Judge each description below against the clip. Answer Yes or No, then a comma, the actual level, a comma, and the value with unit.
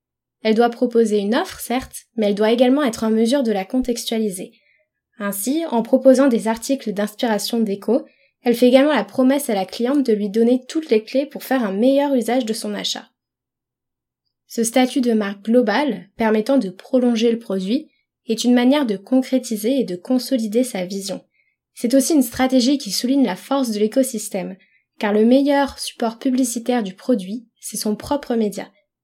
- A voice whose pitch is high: Yes, high, 240 Hz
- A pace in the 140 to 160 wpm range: No, average, 180 wpm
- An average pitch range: Yes, average, 3.3 semitones